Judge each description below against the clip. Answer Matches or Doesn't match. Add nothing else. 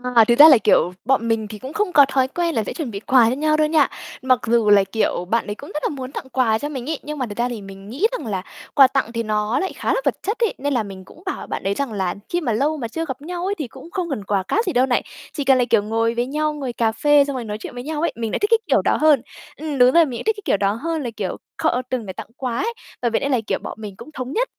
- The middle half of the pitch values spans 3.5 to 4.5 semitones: Doesn't match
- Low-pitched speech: Doesn't match